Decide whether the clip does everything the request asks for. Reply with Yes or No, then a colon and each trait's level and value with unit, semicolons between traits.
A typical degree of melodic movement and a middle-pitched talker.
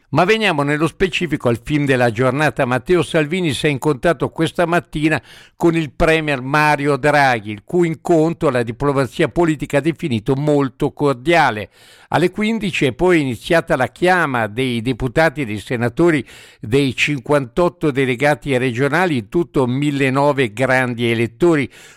Yes: average, 4.1 semitones; medium, 145 Hz